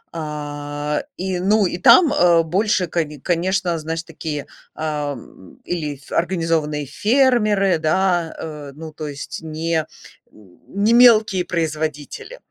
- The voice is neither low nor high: Yes, medium, 165 Hz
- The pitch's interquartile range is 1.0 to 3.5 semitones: No, average, 3.9 semitones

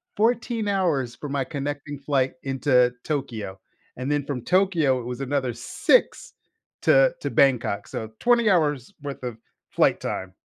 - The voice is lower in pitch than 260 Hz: Yes, medium, 140 Hz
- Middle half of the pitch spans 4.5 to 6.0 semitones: Yes, average, 4.8 semitones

